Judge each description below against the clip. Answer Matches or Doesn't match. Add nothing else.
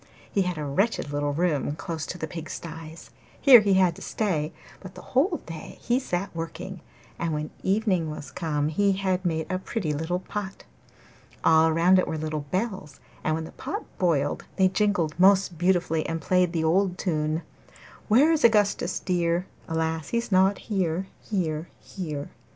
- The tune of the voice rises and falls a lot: Doesn't match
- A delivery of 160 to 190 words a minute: Matches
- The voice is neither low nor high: Matches